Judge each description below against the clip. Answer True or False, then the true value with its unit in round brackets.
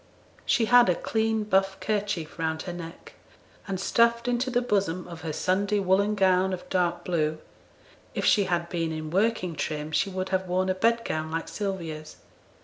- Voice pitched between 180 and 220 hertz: True (185 Hz)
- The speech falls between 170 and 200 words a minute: True (175 wpm)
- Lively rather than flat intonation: False (3.7 semitones)